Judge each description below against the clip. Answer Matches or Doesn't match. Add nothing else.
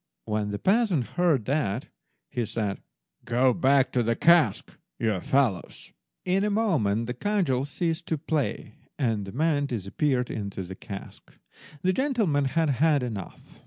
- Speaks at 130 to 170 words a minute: Matches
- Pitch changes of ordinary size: Doesn't match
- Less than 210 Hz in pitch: Matches